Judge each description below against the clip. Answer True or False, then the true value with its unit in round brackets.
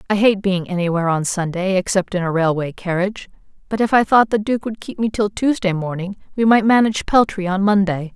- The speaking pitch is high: True (195 Hz)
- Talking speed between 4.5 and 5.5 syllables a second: False (5.8 syllables/s)